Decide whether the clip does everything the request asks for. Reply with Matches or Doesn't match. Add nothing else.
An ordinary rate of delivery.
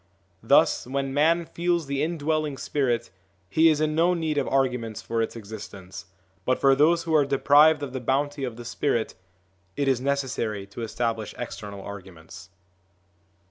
Matches